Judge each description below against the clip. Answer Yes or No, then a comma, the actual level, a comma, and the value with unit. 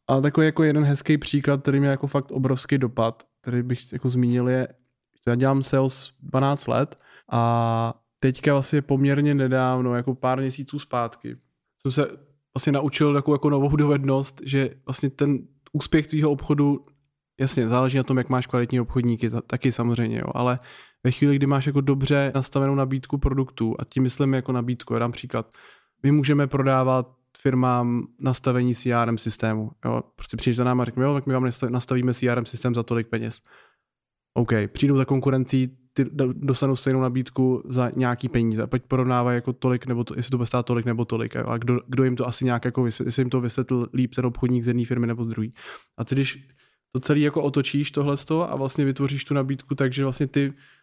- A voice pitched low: Yes, low, 130 Hz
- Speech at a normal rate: No, fast, 195 wpm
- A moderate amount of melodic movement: No, narrow, 2.2 semitones